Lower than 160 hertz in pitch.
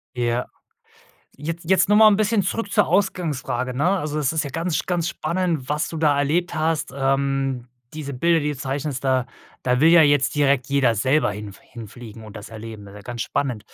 Yes: medium, 140 Hz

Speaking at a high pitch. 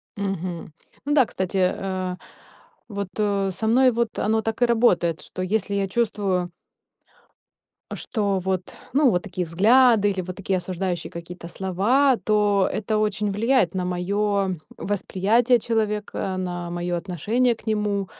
Yes: high, 200 Hz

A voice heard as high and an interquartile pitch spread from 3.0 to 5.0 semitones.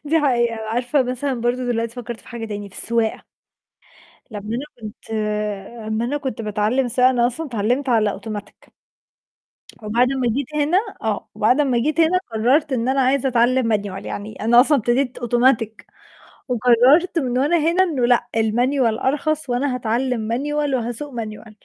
Yes: high, 245 Hz; average, 3.4 semitones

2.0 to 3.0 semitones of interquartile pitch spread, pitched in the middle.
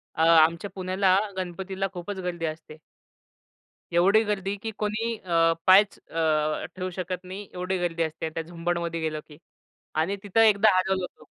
Yes: average, 2.7 semitones; medium, 180 Hz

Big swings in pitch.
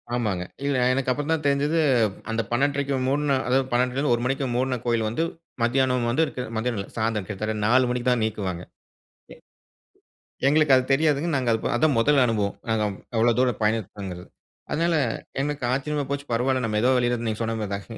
No: average, 3.8 semitones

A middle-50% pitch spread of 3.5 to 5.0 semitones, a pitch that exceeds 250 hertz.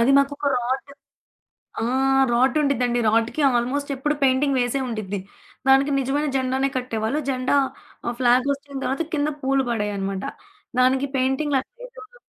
No: narrow, 2.6 semitones; very high, 265 Hz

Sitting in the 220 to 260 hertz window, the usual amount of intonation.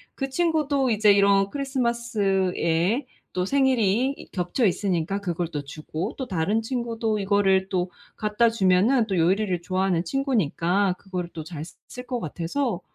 No: high, 200 Hz; average, 4.8 semitones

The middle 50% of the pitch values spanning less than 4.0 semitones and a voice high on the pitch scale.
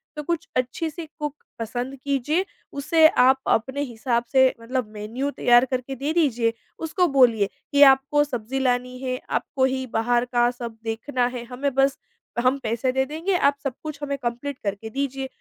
Yes: average, 2.7 semitones; very high, 260 Hz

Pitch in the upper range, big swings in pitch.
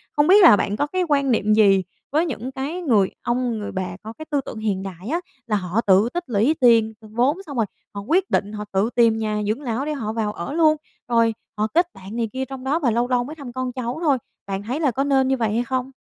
No: high, 240 Hz; average, 4.7 semitones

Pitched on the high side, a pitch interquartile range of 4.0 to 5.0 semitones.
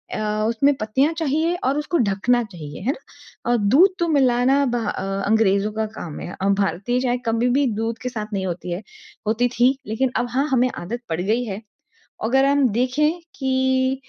Yes: high, 240 Hz; average, 4.3 semitones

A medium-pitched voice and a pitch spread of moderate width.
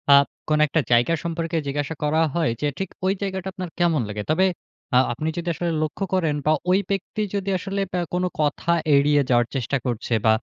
Yes: medium, 160 Hz; average, 4.3 semitones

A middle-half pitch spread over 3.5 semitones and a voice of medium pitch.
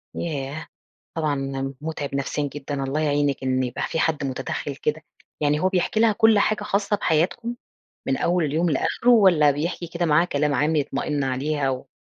Yes: average, 3.9 semitones; medium, 150 Hz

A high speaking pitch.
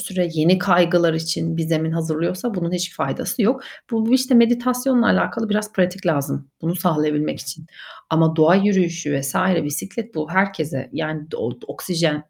No: medium, 170 Hz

